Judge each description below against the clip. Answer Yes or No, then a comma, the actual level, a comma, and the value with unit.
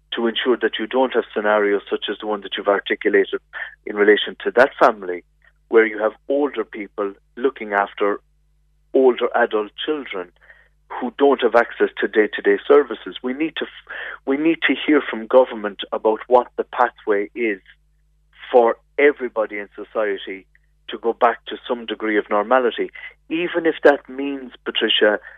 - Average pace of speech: Yes, average, 160 wpm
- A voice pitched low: Yes, low, 130 Hz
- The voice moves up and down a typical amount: No, wide, 7.1 semitones